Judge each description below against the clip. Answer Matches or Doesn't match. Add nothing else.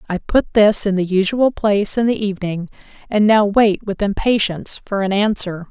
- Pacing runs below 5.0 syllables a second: Doesn't match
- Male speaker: Doesn't match